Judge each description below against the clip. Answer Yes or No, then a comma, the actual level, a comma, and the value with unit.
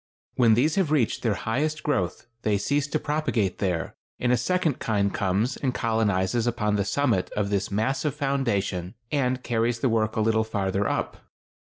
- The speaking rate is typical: Yes, average, 175 wpm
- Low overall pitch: Yes, low, 115 Hz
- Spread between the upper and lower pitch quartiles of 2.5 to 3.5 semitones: No, average, 4.9 semitones